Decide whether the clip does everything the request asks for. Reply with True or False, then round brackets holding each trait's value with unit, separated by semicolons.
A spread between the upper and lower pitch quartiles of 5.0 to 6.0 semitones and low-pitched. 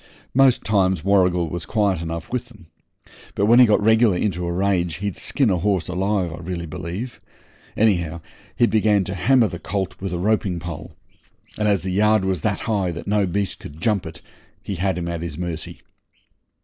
False (3.4 semitones; 95 Hz)